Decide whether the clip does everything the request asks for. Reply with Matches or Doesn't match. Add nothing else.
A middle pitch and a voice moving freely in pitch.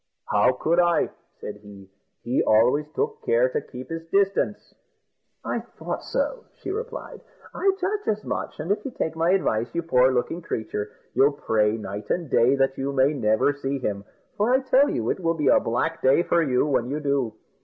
Matches